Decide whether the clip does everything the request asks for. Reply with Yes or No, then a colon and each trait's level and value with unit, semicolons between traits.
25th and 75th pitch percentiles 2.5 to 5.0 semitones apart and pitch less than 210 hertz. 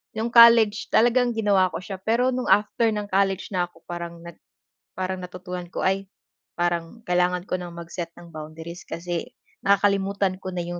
Yes: average, 3.0 semitones; medium, 185 Hz